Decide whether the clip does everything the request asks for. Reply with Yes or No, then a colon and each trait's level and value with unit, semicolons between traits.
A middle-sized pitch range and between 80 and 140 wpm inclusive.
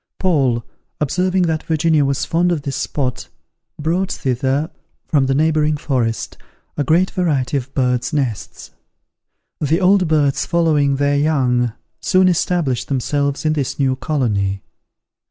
Yes: average, 3.6 semitones; slow, 135 wpm